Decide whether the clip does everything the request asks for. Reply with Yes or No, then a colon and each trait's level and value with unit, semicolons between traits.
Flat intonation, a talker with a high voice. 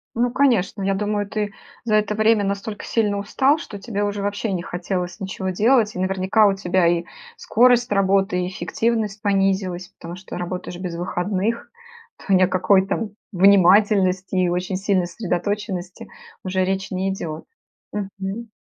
Yes: narrow, 2.3 semitones; high, 195 Hz